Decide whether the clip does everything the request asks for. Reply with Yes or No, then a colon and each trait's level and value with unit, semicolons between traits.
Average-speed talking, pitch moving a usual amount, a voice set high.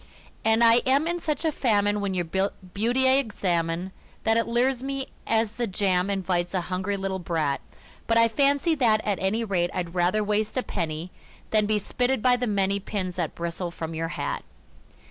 Yes: average, 190 wpm; average, 4.4 semitones; high, 205 Hz